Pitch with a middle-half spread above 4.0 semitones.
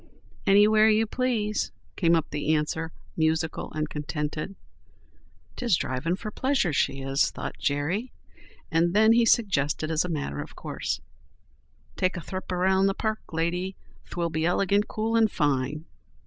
Yes: wide, 5.5 semitones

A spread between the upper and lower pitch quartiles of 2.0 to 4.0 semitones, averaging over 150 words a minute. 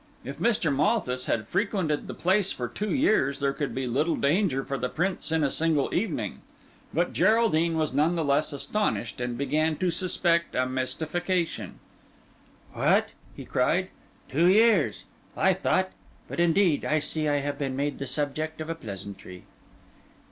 No: average, 4.5 semitones; average, 160 wpm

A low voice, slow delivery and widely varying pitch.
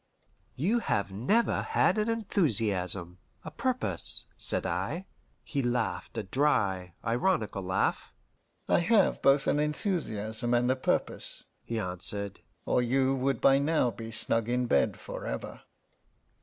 Yes: low, 125 Hz; slow, 130 wpm; wide, 6.4 semitones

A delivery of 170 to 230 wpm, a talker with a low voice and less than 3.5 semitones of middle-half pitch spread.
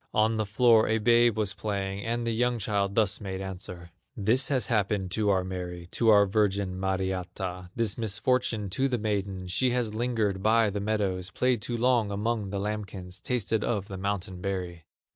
Yes: average, 180 wpm; low, 105 Hz; average, 3.0 semitones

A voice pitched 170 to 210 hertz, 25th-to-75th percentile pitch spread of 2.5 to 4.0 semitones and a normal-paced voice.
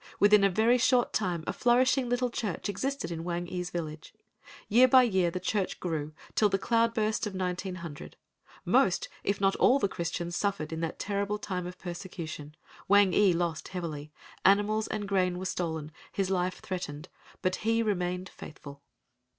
Yes: medium, 185 Hz; average, 3.4 semitones; average, 160 wpm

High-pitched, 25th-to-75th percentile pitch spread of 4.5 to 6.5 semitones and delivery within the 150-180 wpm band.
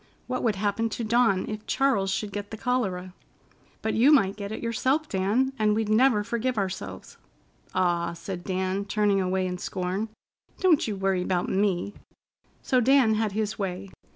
No: high, 205 Hz; average, 3.4 semitones; average, 170 wpm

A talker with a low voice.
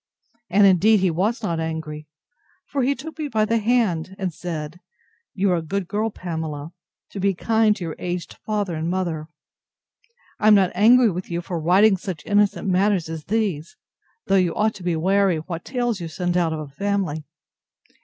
No: medium, 185 Hz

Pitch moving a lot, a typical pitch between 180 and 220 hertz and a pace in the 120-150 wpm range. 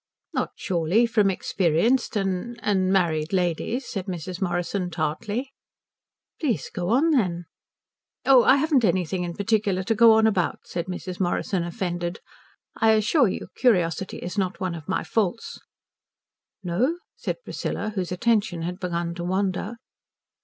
No: average, 4.2 semitones; high, 190 Hz; average, 140 wpm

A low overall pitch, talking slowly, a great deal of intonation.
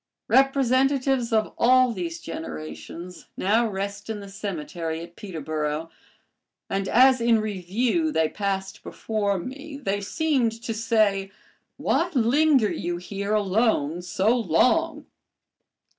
No: high, 210 Hz; slow, 115 wpm; wide, 5.7 semitones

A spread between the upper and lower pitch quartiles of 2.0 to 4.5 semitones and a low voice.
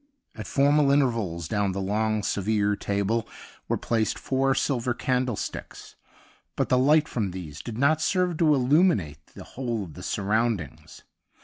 No: average, 5.1 semitones; low, 115 Hz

